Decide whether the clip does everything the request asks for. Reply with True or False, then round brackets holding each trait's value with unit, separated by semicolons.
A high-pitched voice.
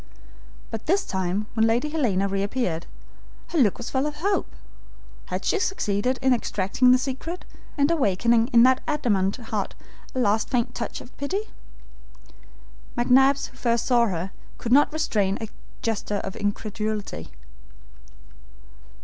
True (235 Hz)